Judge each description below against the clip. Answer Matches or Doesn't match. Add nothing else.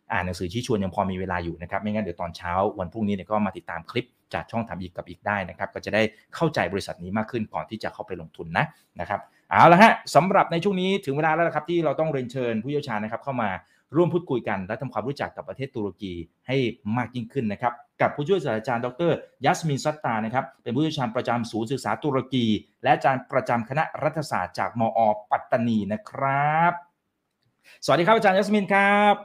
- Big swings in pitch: Matches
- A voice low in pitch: Matches